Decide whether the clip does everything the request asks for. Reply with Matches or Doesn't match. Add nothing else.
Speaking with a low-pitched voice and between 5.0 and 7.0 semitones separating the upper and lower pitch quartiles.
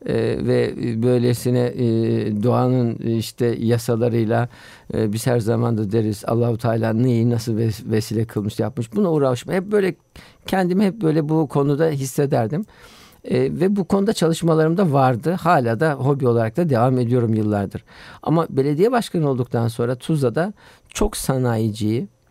Matches